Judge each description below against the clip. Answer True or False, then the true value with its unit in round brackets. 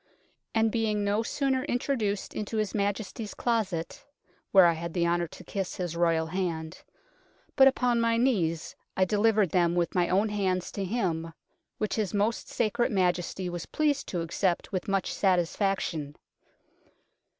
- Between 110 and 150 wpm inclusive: False (160 wpm)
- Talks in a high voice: True (195 Hz)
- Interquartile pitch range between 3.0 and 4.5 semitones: True (4.1 semitones)